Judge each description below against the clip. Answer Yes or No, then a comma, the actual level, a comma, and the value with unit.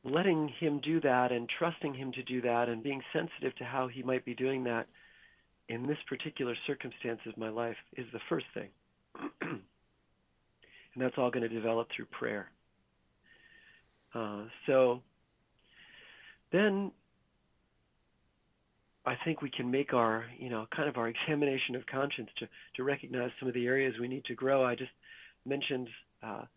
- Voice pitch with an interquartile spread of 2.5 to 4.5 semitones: Yes, average, 3.2 semitones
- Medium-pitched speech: No, low, 130 Hz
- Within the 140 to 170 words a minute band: Yes, average, 160 wpm